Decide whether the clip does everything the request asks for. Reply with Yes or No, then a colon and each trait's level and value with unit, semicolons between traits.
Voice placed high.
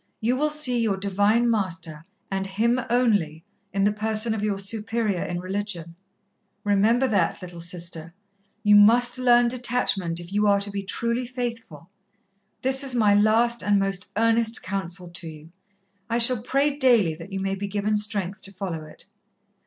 Yes: high, 205 Hz